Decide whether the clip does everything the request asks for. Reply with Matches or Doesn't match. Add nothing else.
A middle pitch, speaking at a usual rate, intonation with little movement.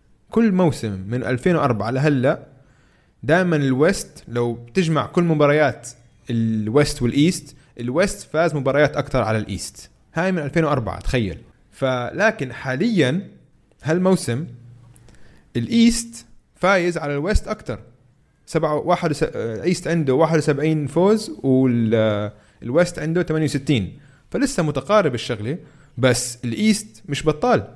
Doesn't match